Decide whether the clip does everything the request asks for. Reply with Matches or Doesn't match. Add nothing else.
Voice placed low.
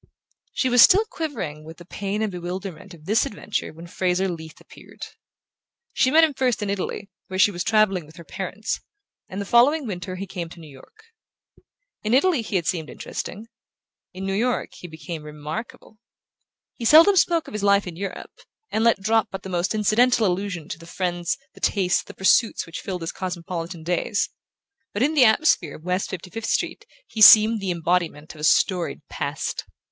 Doesn't match